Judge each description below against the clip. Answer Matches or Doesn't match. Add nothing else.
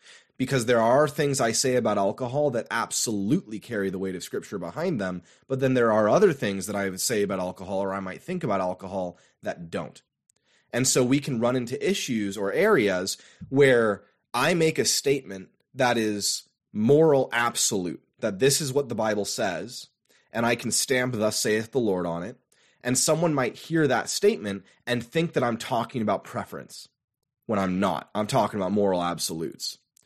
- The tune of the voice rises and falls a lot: Matches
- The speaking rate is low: Doesn't match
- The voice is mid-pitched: Doesn't match